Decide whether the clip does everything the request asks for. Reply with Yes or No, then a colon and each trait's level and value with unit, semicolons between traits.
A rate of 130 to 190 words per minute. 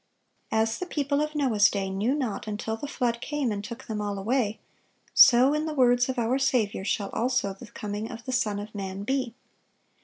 No: fast, 205 wpm